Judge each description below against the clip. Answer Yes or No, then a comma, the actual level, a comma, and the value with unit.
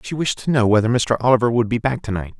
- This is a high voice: No, low, 115 Hz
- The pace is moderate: No, fast, 300 wpm